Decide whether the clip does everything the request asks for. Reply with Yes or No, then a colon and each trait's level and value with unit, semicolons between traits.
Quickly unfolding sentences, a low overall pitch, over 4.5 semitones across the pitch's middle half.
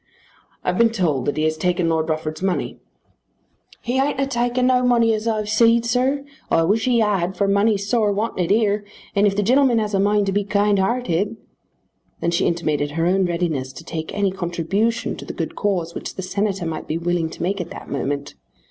No: fast, 210 wpm; high, 200 Hz; average, 4.9 semitones